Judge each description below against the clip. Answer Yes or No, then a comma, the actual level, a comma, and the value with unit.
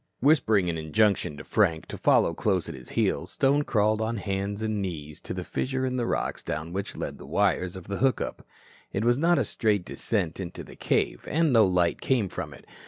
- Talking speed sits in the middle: No, fast, 220 wpm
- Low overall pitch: Yes, low, 100 Hz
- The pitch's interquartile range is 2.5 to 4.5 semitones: No, average, 5.0 semitones